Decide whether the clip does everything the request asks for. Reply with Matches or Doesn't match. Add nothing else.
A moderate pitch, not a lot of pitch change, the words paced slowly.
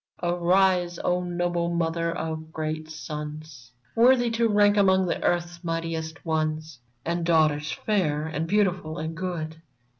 Matches